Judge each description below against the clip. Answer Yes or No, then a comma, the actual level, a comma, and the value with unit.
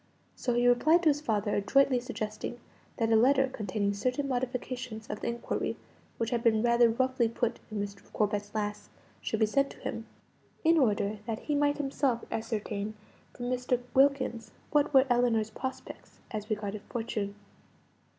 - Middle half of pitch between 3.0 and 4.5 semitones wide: Yes, average, 3.3 semitones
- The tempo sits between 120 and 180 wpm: Yes, average, 160 wpm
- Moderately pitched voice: No, high, 235 Hz